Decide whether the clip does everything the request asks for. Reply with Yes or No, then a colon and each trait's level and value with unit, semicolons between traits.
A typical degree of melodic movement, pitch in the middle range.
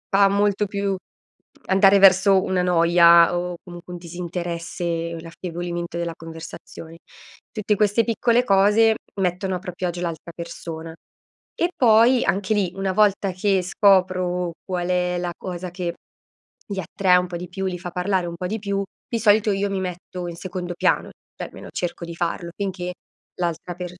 No: narrow, 2.3 semitones; medium, 180 Hz